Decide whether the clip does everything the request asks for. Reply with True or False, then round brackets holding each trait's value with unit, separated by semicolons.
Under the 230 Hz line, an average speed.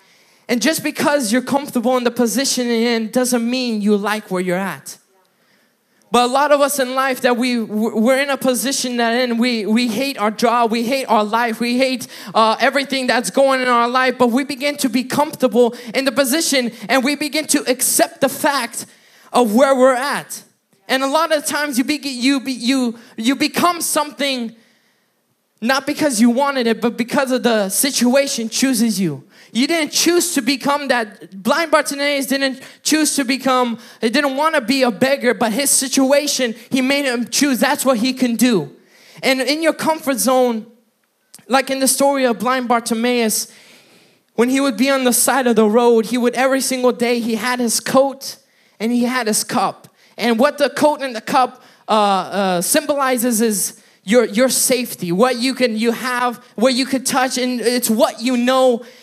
False (255 Hz; 195 wpm)